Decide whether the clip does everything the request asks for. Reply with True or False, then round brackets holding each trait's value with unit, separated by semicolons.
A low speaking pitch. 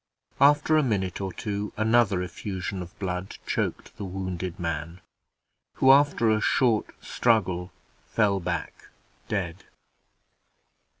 True (100 Hz)